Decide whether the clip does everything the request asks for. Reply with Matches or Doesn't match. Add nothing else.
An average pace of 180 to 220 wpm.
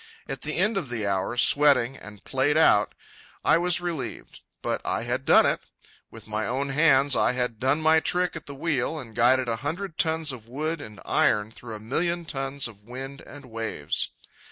Matches